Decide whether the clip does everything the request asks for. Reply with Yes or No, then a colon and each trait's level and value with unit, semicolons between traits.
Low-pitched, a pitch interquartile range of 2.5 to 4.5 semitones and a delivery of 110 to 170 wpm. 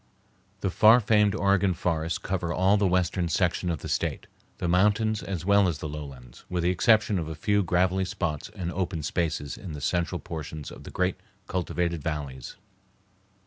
No: very low, 90 Hz; average, 3.4 semitones; average, 180 wpm